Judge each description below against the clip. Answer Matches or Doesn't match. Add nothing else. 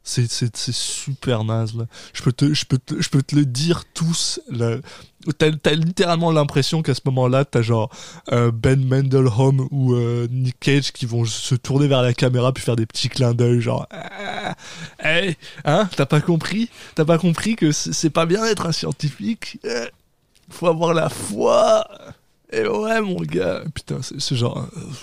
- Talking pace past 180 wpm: Doesn't match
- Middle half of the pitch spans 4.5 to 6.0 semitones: Matches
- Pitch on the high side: Doesn't match